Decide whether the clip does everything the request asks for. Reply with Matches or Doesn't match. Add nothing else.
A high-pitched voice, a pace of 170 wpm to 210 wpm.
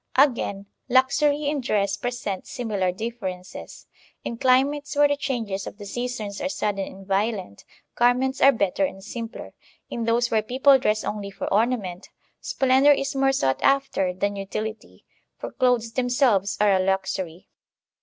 Doesn't match